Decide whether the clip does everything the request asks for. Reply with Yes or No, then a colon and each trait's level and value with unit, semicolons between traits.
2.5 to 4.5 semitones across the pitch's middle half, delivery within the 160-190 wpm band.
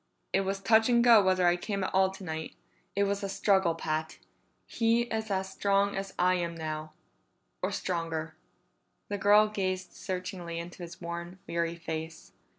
Yes: average, 2.9 semitones; average, 165 wpm